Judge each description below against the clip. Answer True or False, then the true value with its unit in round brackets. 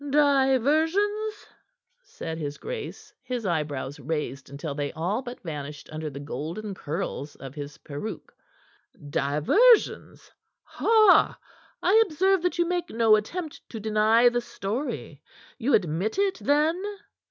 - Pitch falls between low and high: False (220 Hz)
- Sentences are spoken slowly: True (125 wpm)